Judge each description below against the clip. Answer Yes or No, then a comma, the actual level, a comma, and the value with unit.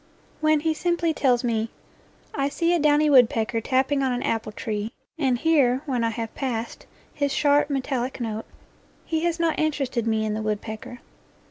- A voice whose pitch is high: Yes, very high, 260 Hz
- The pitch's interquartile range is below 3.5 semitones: No, average, 4.5 semitones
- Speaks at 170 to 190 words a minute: Yes, average, 180 wpm